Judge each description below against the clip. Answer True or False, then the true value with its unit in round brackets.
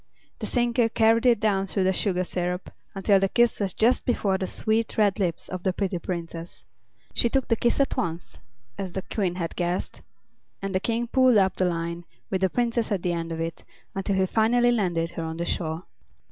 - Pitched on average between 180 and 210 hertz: True (190 Hz)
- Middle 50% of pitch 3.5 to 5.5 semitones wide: True (4.3 semitones)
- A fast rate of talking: True (210 wpm)